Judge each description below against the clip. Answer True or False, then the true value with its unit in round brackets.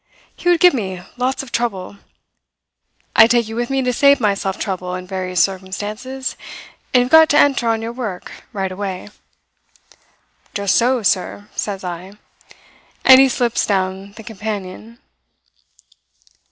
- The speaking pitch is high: True (215 Hz)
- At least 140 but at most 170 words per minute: True (145 wpm)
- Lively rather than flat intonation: False (4.6 semitones)